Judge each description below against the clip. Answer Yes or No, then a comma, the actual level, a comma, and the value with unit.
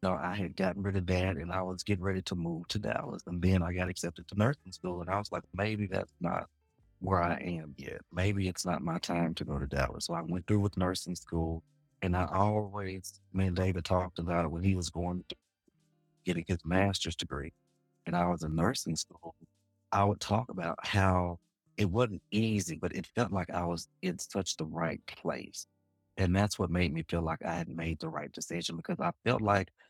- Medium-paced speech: No, fast, 225 wpm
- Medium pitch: No, very low, 95 Hz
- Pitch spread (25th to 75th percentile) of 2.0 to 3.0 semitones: Yes, narrow, 2.4 semitones